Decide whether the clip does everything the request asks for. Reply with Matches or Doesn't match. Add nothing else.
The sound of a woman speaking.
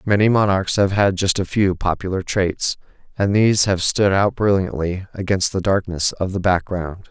Doesn't match